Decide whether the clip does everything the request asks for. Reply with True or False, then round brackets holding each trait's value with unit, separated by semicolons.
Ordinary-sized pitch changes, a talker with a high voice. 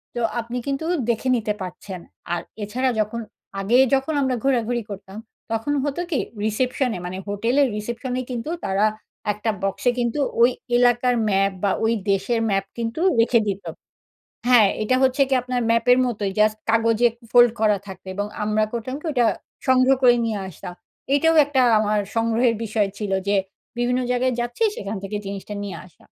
True (3.3 semitones; 230 Hz)